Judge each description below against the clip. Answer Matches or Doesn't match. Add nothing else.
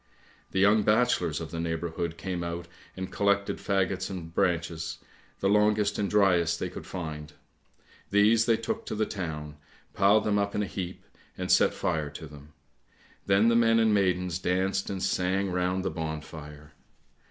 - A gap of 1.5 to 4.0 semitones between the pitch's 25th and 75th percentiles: Matches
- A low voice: Matches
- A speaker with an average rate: Matches